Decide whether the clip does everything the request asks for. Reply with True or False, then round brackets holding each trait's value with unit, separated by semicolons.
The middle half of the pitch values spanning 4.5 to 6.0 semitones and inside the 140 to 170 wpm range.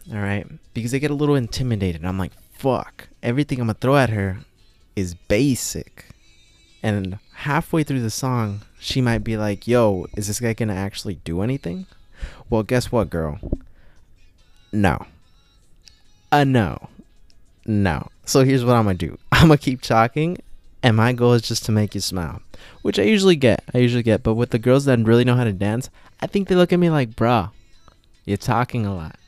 False (4.9 semitones; 195 wpm)